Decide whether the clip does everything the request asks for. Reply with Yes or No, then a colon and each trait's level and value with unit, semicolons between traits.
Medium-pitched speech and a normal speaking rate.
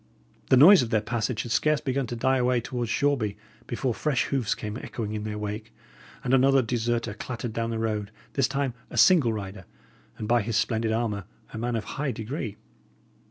No: low, 115 Hz; average, 195 wpm